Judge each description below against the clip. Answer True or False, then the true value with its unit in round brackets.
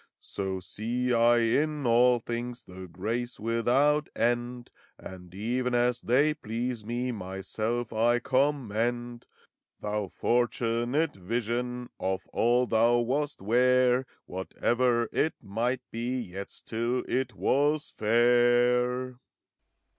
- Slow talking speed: True (110 wpm)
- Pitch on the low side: True (120 Hz)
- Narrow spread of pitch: True (1.8 semitones)